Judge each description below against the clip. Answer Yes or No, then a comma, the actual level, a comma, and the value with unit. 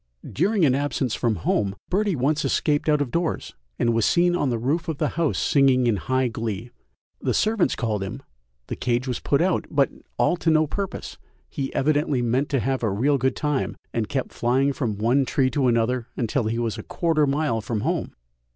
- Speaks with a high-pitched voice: No, low, 135 Hz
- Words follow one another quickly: Yes, fast, 210 wpm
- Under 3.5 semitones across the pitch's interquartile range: No, average, 4.2 semitones